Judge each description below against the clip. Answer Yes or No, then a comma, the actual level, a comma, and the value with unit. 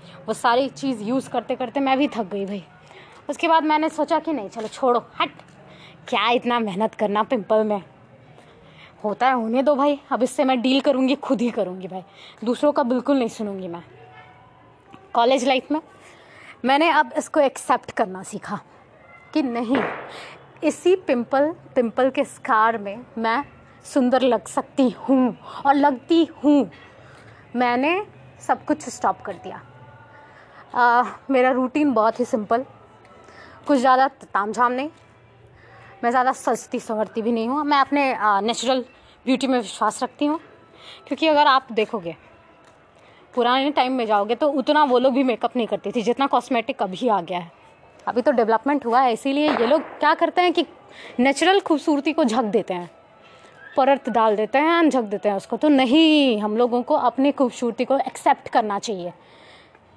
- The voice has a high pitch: Yes, very high, 255 Hz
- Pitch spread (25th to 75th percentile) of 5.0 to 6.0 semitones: No, average, 4.2 semitones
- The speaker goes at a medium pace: Yes, average, 160 wpm